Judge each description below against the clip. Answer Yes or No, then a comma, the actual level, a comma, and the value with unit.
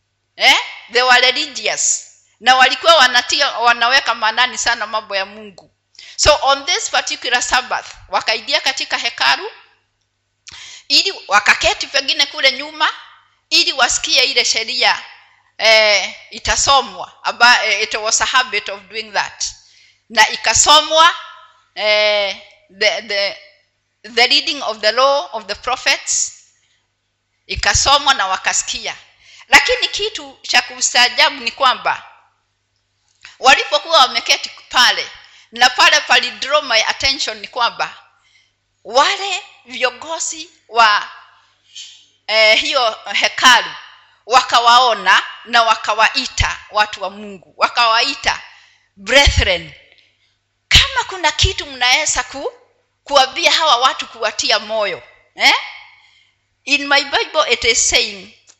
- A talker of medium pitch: No, very high, 255 Hz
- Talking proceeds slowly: Yes, slow, 95 wpm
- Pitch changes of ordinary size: No, wide, 5.7 semitones